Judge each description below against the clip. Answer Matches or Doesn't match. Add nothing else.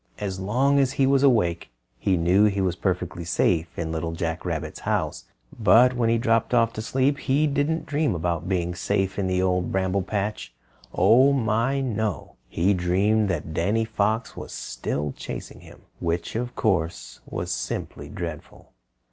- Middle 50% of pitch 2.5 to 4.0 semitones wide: Doesn't match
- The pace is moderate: Matches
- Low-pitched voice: Matches